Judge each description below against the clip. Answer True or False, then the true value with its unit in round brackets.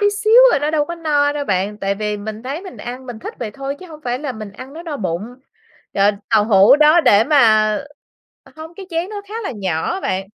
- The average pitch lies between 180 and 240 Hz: False (260 Hz)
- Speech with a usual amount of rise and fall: False (7.0 semitones)